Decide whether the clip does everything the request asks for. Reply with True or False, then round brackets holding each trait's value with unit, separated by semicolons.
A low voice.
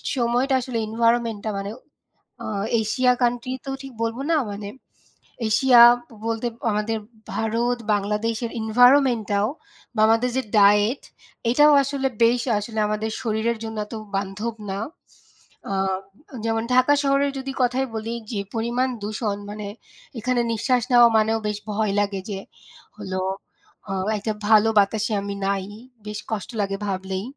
False (225 Hz)